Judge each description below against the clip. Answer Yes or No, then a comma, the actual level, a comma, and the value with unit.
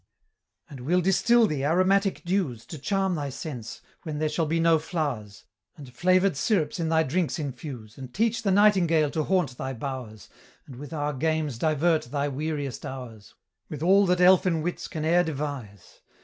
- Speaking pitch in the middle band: Yes, medium, 155 Hz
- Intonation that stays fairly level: No, average, 5.0 semitones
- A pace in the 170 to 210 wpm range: Yes, average, 175 wpm